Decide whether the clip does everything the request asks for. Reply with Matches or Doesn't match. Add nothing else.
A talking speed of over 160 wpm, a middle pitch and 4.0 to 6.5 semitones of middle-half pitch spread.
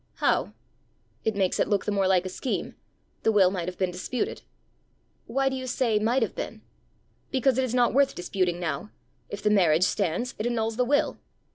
Doesn't match